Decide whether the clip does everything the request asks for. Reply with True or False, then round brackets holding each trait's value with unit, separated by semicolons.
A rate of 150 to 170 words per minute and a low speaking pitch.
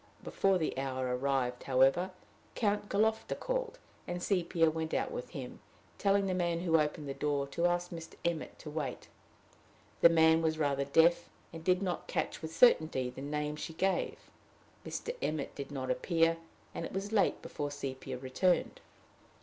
False (165 wpm; 160 Hz)